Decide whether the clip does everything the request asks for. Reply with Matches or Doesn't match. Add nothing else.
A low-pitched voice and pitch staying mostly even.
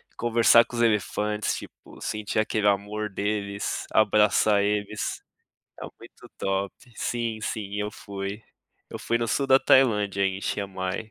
Matches